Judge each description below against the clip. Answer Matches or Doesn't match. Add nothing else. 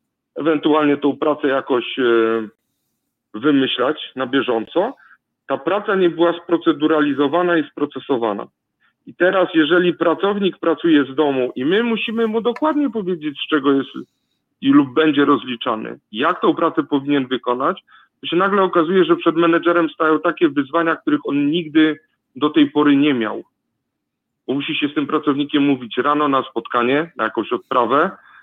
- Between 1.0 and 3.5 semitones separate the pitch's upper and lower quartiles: Matches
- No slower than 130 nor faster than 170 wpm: Matches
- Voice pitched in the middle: Matches